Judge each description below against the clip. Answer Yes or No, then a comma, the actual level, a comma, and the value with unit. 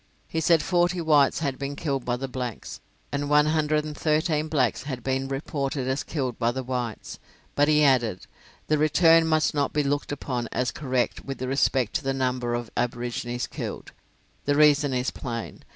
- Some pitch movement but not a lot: Yes, average, 3.1 semitones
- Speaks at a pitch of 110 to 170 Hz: Yes, medium, 140 Hz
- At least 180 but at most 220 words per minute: Yes, average, 185 wpm